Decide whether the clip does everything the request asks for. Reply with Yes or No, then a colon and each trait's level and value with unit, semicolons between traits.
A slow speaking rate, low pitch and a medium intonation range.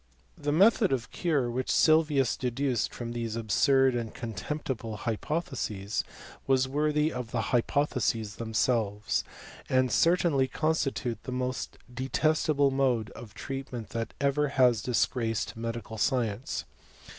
Yes: slow, 120 wpm; low, 125 Hz; average, 3.6 semitones